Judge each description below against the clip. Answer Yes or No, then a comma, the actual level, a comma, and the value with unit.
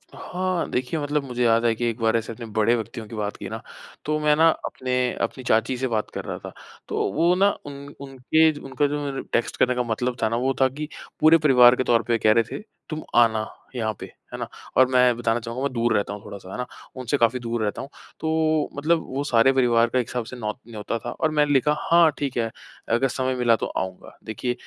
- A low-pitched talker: Yes, low, 125 Hz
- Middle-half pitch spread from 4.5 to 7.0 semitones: No, average, 3.9 semitones